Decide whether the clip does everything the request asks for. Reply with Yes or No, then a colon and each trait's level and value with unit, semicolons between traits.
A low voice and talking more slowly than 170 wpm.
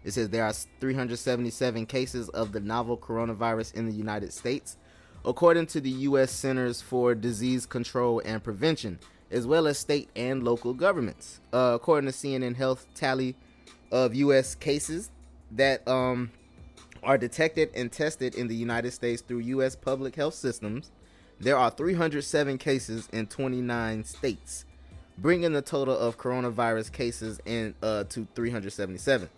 Yes: low, 120 Hz; average, 145 wpm